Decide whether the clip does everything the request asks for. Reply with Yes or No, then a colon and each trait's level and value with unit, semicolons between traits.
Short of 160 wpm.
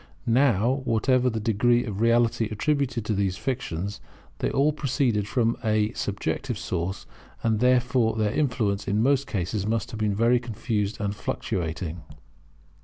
Yes: average, 145 wpm